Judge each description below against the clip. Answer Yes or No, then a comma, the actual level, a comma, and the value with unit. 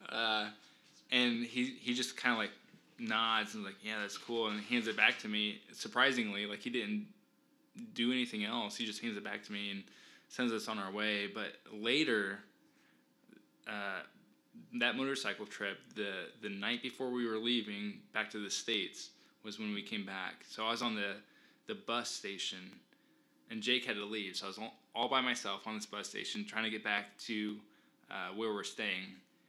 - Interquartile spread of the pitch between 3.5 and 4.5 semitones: No, average, 3.0 semitones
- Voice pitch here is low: Yes, low, 110 Hz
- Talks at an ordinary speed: Yes, average, 195 wpm